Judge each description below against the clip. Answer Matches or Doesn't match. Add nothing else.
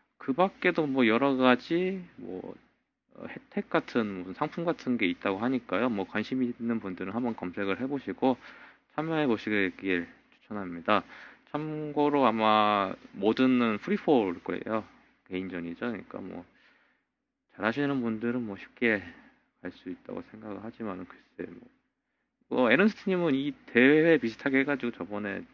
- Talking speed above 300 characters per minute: Doesn't match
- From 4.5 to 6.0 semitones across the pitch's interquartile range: Doesn't match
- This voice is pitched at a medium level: Doesn't match